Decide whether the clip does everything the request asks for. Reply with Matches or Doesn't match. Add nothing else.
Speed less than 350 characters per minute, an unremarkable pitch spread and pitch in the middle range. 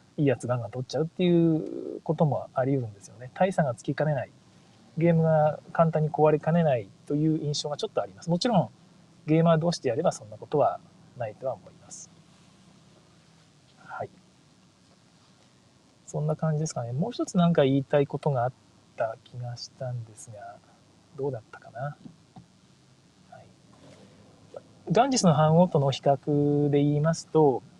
Matches